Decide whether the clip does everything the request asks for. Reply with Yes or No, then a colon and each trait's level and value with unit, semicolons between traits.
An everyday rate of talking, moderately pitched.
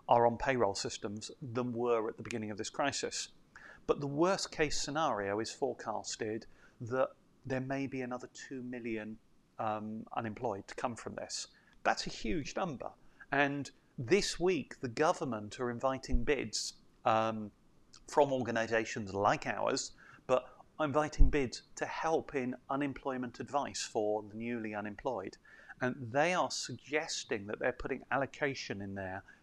No: average, 145 wpm; low, 125 Hz